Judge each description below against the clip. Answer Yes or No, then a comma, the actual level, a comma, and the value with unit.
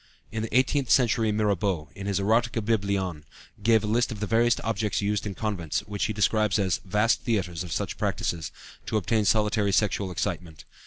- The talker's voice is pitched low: Yes, low, 105 Hz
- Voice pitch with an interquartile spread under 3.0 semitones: Yes, narrow, 2.6 semitones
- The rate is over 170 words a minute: Yes, average, 180 wpm